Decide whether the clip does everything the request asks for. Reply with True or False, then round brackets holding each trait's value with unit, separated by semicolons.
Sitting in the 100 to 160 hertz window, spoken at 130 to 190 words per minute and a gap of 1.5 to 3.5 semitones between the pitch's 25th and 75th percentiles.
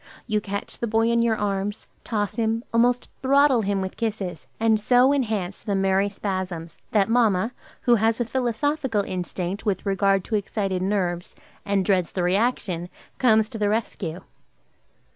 False (210 Hz; 160 wpm; 3.2 semitones)